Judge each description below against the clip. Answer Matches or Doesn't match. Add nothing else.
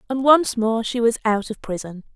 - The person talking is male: Doesn't match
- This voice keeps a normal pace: Doesn't match